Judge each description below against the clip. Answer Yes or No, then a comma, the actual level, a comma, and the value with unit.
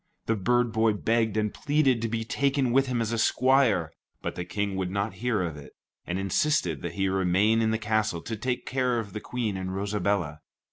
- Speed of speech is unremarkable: No, fast, 215 wpm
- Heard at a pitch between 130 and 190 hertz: No, low, 110 Hz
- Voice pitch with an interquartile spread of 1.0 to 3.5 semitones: No, average, 4.0 semitones